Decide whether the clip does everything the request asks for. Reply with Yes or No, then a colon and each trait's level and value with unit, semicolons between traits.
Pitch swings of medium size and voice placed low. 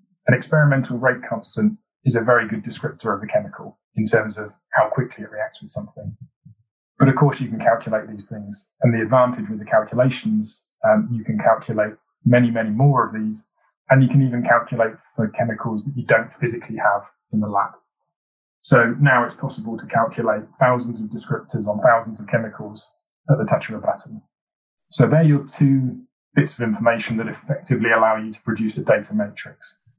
Yes: average, 4.5 semitones; low, 120 Hz